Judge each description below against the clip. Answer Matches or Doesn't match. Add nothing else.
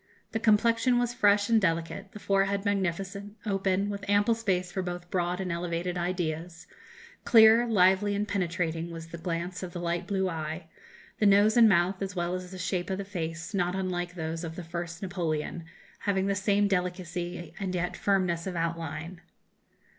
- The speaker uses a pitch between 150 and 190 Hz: Matches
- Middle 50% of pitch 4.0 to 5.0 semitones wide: Doesn't match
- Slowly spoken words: Doesn't match